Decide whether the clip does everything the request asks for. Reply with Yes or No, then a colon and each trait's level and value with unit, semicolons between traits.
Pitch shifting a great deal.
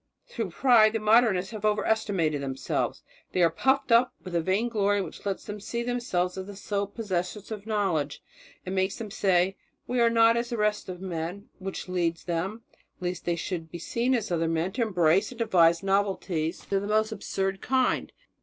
No: average, 3.8 semitones